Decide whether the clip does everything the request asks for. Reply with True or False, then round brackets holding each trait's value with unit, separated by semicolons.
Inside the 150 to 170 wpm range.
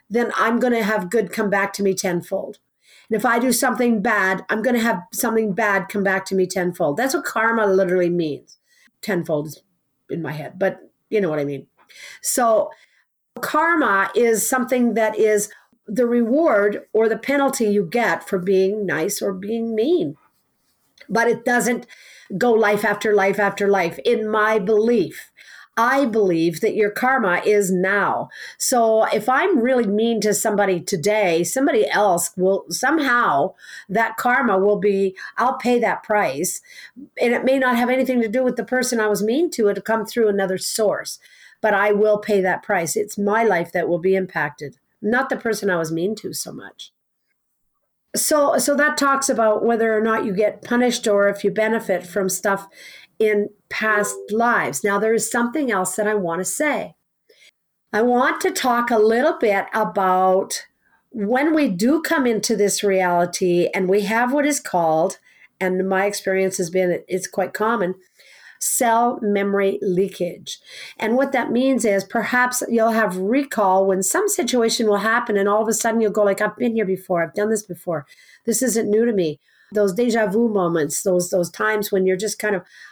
False (185 wpm)